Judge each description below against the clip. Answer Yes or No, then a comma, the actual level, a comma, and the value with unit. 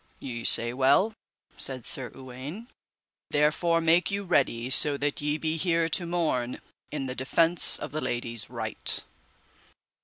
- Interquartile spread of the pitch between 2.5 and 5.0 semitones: Yes, average, 4.5 semitones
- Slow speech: No, average, 145 wpm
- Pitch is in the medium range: Yes, medium, 145 Hz